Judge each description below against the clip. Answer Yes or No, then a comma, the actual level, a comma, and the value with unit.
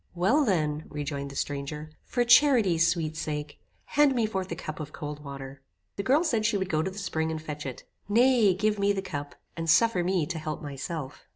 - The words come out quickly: Yes, fast, 210 wpm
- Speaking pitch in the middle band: Yes, medium, 165 Hz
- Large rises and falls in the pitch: Yes, wide, 5.7 semitones